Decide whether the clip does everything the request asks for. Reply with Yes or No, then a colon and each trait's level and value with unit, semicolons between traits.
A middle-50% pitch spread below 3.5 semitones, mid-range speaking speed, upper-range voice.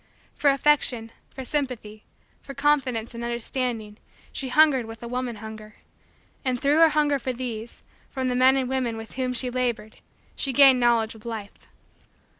Yes: average, 2.9 semitones; average, 165 wpm; very high, 250 Hz